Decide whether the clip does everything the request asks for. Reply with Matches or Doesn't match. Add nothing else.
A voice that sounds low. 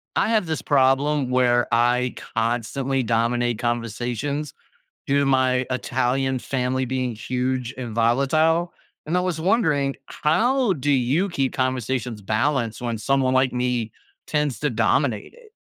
Matches